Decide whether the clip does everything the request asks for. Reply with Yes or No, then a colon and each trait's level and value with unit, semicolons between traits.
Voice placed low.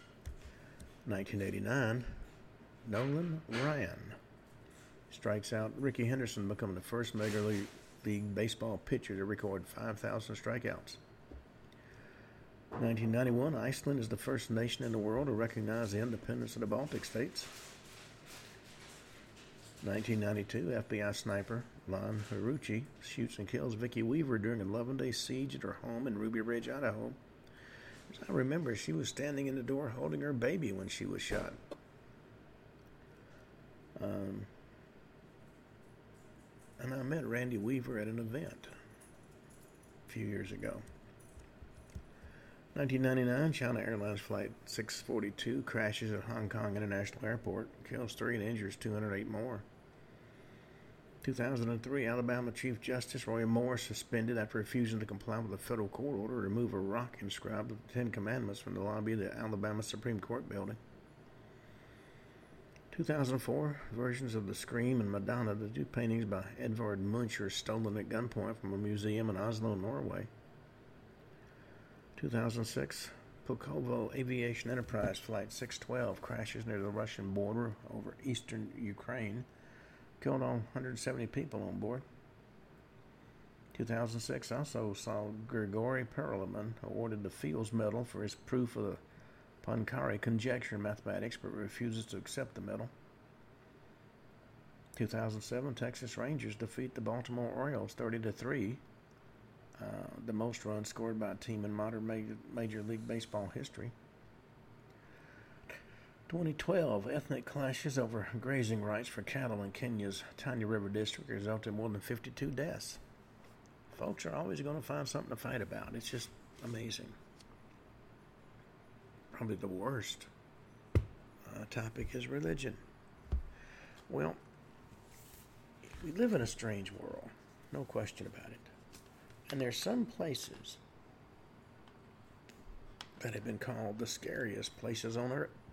Yes: low, 115 Hz